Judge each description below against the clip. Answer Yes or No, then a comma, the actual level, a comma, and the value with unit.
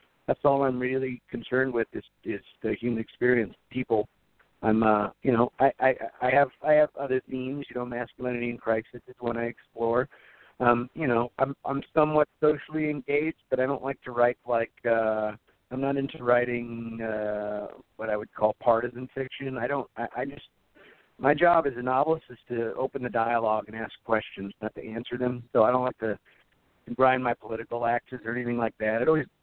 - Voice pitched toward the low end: Yes, low, 120 Hz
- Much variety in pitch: No, average, 2.7 semitones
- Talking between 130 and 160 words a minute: No, average, 200 wpm